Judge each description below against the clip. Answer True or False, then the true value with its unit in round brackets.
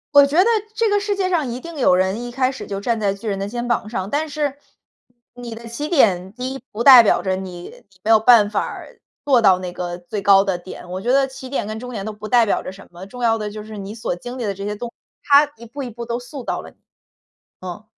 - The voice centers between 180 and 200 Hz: False (230 Hz)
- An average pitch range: True (4.7 semitones)